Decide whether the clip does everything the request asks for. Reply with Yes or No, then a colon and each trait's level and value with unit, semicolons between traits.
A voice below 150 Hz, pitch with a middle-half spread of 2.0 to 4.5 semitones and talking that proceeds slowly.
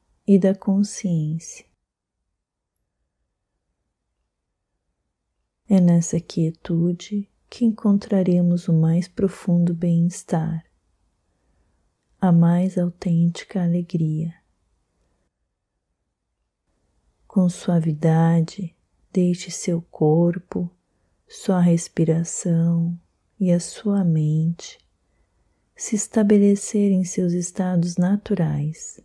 No: medium, 175 Hz; narrow, 2.4 semitones; slow, 70 wpm